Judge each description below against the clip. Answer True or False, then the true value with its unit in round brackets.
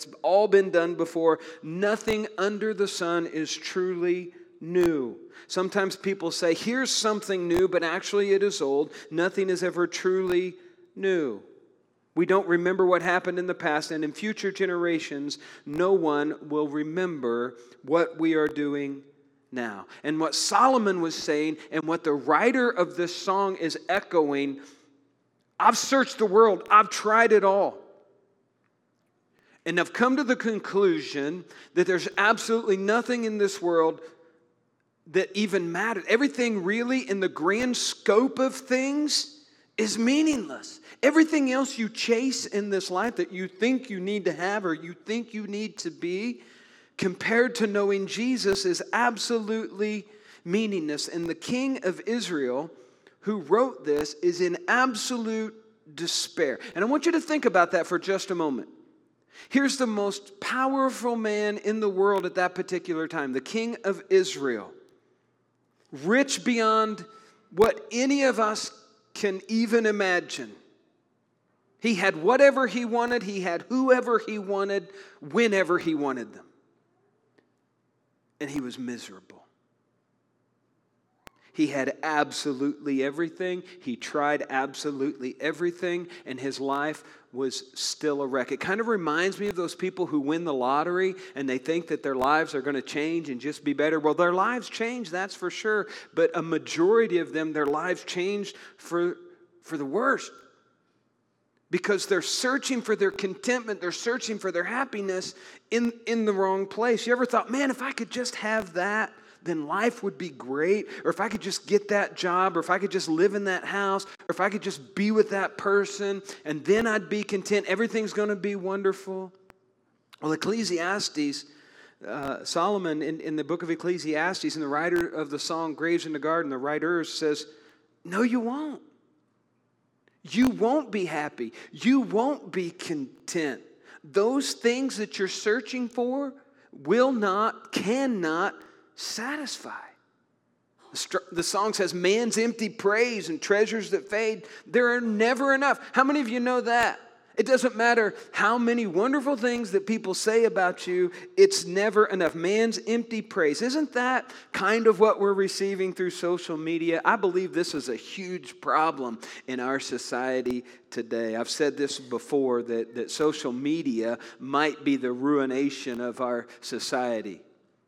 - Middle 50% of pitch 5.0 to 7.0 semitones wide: True (5.6 semitones)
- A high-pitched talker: True (195 Hz)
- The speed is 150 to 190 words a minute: True (155 wpm)